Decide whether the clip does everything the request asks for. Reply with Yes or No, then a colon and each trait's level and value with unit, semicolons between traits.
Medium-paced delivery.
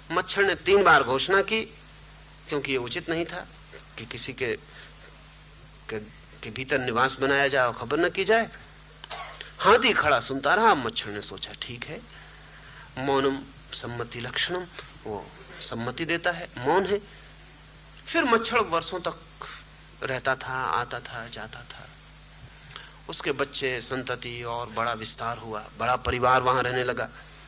Yes: average, 140 wpm